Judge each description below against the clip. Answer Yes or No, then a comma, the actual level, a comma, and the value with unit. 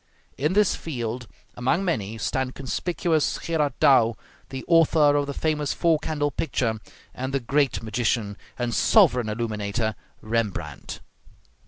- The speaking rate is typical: No, slow, 130 wpm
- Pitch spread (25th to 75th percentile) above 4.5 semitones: Yes, average, 5.0 semitones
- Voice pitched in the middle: No, low, 130 Hz